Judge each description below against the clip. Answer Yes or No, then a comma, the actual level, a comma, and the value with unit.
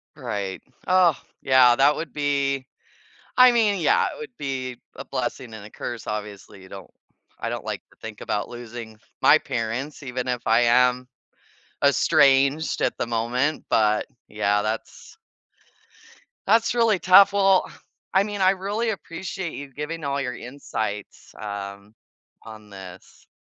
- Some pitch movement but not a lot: No, wide, 7.3 semitones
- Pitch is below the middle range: Yes, low, 130 Hz